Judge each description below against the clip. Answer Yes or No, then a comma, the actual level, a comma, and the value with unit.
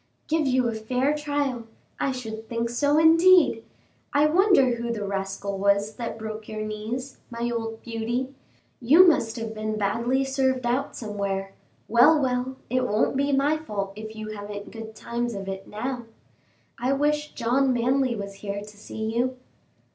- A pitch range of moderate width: Yes, average, 3.8 semitones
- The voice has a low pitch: No, high, 235 Hz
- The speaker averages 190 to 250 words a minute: No, average, 165 wpm